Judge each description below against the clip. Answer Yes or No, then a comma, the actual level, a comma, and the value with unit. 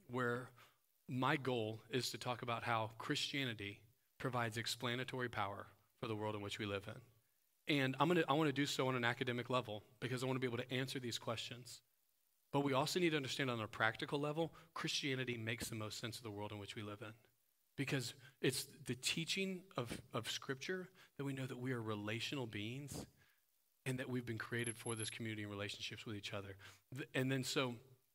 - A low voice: Yes, low, 125 Hz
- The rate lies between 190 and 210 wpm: Yes, fast, 205 wpm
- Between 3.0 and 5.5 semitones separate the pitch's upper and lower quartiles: Yes, average, 3.4 semitones